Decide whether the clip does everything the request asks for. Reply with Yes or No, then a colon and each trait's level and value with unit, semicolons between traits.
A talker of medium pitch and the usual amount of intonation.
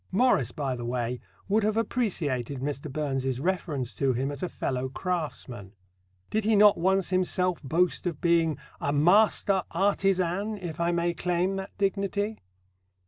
No: medium, 170 Hz; wide, 5.9 semitones